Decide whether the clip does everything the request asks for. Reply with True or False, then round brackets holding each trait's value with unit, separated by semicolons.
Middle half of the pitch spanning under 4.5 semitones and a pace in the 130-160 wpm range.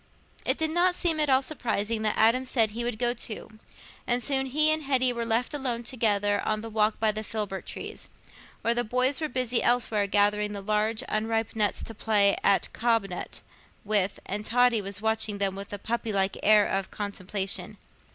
False (3.1 semitones; 190 wpm)